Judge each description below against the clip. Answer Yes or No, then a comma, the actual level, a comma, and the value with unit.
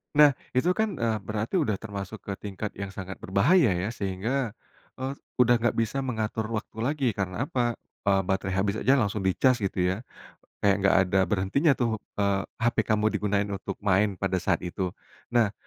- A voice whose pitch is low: Yes, low, 105 Hz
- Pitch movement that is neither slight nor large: Yes, average, 3.8 semitones